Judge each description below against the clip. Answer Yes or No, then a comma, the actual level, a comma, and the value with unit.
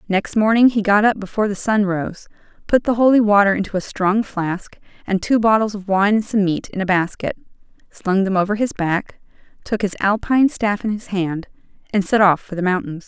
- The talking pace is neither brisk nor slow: No, fast, 210 wpm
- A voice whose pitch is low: No, high, 200 Hz